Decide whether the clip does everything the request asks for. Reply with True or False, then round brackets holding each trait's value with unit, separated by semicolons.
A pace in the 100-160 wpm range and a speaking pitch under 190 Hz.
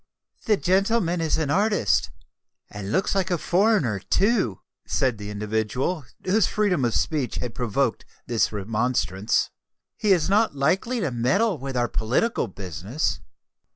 True (140 wpm; 140 Hz)